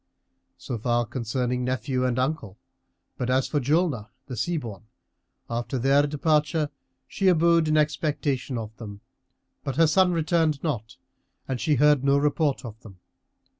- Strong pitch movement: No, average, 4.2 semitones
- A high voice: No, low, 135 Hz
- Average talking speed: Yes, average, 150 wpm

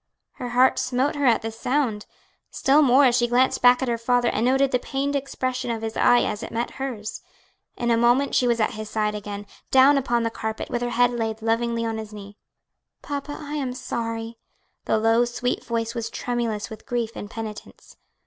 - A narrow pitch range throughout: Yes, narrow, 2.2 semitones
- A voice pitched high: Yes, high, 240 Hz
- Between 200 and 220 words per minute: Yes, fast, 205 wpm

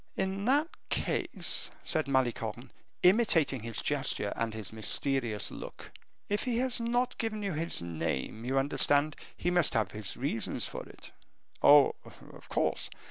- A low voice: No, medium, 145 Hz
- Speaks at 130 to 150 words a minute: Yes, average, 145 wpm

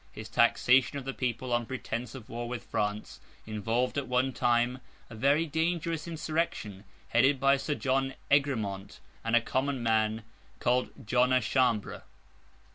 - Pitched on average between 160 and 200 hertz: No, low, 125 Hz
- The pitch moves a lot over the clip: No, average, 3.1 semitones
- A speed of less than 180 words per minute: Yes, average, 150 wpm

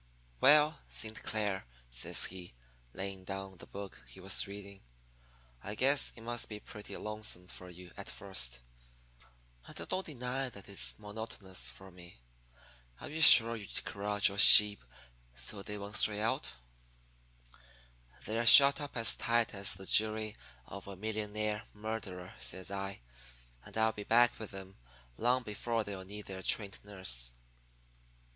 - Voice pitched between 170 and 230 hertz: No, low, 105 Hz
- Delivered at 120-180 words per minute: Yes, average, 150 wpm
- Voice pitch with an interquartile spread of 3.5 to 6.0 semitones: No, narrow, 2.6 semitones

